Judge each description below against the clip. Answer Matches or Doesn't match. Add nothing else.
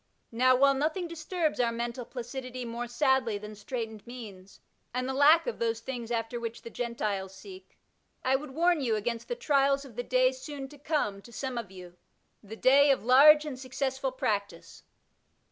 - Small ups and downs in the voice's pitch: Doesn't match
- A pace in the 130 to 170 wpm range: Doesn't match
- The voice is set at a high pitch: Matches